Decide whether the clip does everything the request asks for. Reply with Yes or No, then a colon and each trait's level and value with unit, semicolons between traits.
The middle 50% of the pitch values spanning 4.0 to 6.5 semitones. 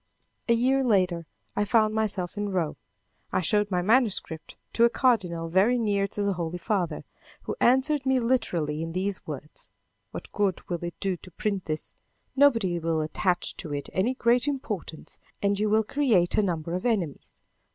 Yes: average, 5.0 semitones